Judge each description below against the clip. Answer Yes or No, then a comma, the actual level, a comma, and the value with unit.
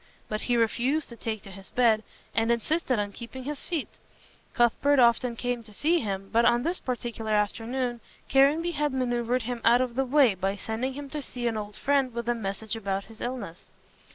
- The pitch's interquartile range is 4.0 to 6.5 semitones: No, average, 3.1 semitones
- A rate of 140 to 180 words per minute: No, average, 200 wpm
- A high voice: Yes, high, 240 Hz